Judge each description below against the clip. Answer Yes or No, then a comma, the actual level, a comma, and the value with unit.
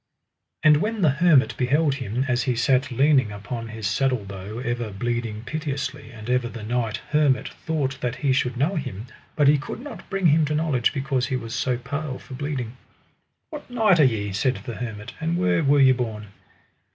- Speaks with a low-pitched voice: Yes, low, 130 Hz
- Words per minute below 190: No, average, 195 wpm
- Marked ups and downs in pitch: No, average, 4.3 semitones